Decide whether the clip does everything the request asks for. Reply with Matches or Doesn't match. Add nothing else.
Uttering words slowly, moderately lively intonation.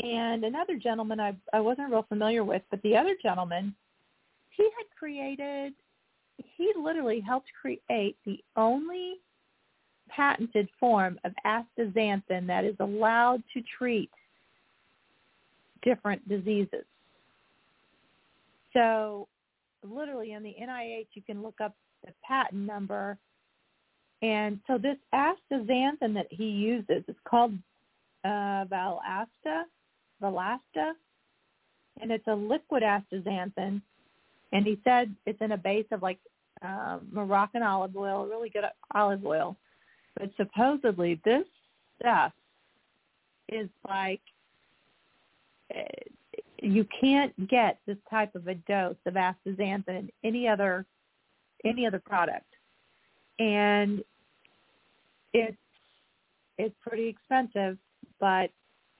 Matches